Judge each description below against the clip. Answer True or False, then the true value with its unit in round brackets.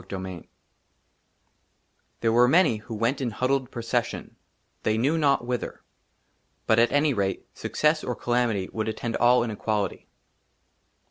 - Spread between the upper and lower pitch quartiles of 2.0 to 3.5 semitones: True (2.8 semitones)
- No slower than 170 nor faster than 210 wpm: False (145 wpm)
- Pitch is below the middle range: True (120 Hz)